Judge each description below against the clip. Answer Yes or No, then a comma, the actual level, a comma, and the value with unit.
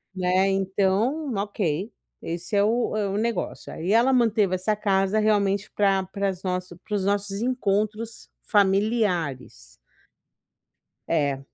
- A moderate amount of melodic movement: No, narrow, 2.2 semitones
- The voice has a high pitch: Yes, high, 200 Hz